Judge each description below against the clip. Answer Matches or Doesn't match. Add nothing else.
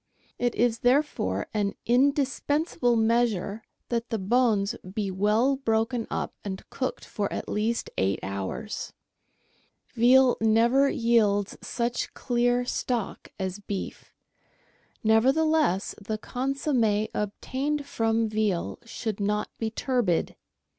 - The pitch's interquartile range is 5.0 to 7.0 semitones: Doesn't match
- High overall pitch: Matches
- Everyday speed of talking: Doesn't match